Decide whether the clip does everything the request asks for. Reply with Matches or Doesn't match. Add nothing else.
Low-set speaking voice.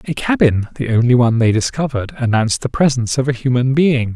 Matches